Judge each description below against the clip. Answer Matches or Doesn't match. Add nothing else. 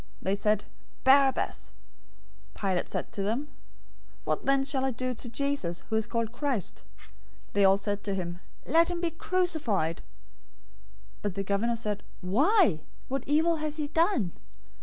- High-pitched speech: Matches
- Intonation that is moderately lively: Doesn't match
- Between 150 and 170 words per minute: Matches